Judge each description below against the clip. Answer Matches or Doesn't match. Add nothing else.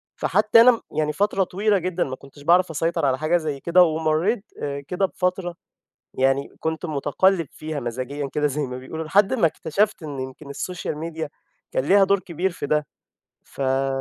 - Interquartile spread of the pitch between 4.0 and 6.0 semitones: Matches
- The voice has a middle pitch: Matches